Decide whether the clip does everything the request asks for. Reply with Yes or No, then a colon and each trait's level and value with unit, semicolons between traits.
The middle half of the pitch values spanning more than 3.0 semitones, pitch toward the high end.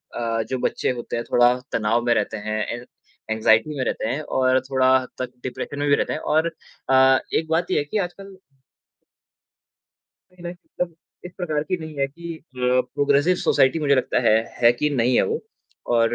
No: average, 4.7 semitones; low, 135 Hz